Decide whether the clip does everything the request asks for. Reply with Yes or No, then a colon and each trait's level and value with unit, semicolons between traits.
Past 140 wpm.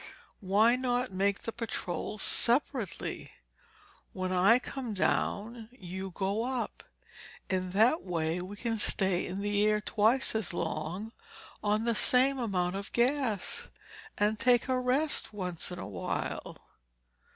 No: slow, 135 wpm